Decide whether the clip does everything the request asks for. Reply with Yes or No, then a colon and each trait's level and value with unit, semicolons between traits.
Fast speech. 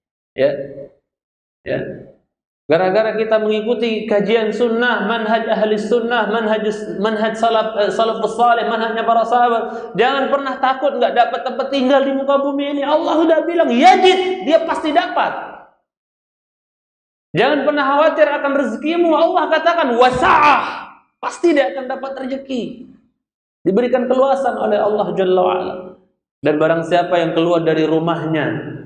No: average, 130 wpm